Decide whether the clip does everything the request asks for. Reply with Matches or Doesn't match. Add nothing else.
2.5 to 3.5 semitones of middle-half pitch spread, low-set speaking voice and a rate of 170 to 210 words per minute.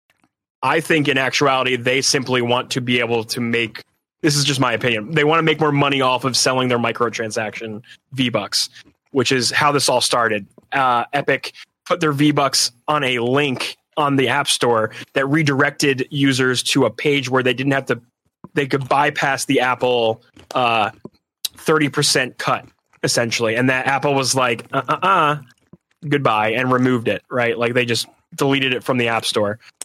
Matches